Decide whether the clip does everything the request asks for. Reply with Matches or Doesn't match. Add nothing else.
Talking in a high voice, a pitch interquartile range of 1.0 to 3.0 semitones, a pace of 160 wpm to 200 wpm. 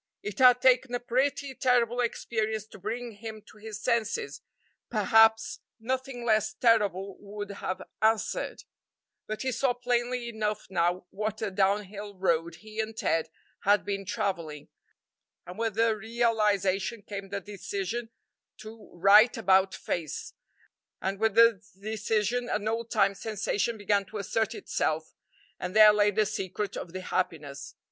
Doesn't match